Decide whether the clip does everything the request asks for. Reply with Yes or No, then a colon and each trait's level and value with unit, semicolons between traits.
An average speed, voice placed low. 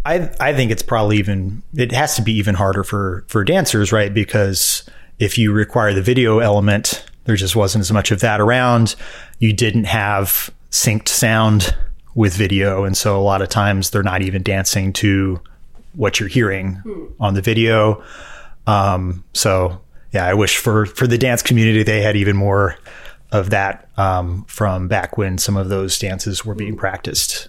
Yes: average, 180 wpm; low, 105 Hz